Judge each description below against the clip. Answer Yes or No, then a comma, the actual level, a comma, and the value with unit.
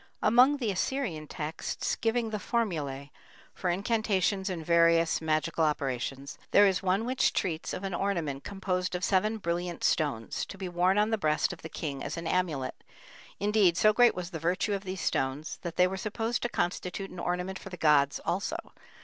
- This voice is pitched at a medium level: Yes, medium, 180 Hz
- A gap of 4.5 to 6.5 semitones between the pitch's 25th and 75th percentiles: No, average, 4.1 semitones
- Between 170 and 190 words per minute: Yes, average, 185 wpm